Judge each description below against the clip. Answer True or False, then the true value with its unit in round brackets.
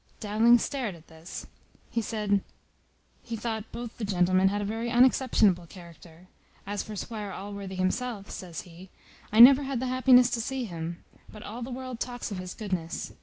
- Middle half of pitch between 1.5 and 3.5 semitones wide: False (4.5 semitones)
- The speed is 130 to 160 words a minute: False (175 wpm)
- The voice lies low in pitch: False (210 Hz)